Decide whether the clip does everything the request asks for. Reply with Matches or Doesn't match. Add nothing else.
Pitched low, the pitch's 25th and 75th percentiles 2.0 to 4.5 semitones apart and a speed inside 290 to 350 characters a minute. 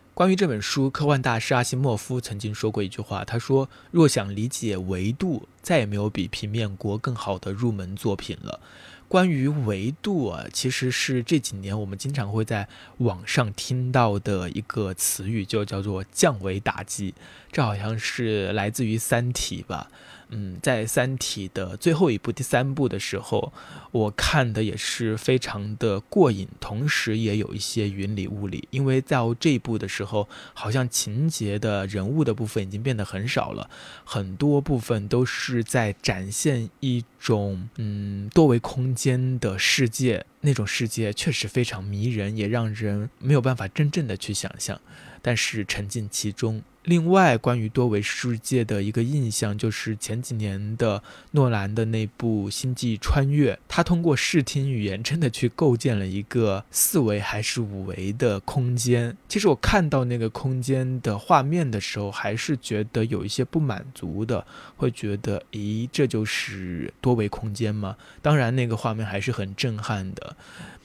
Doesn't match